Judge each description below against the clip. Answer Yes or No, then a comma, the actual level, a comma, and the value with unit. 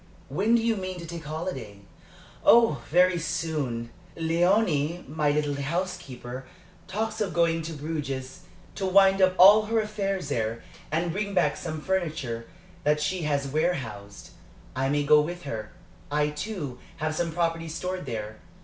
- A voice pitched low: No, medium, 160 Hz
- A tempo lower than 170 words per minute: Yes, average, 155 wpm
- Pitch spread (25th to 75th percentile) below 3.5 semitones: No, average, 4.7 semitones